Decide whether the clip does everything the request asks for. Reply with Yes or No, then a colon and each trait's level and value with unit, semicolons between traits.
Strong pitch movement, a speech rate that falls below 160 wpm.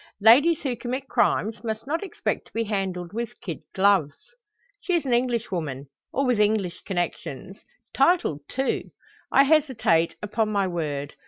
Yes: wide, 6.5 semitones; average, 150 wpm